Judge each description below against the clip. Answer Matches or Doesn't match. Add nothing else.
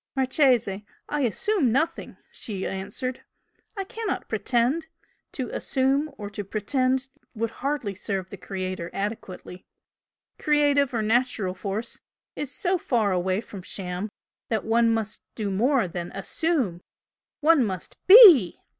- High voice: Matches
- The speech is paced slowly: Matches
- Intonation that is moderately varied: Doesn't match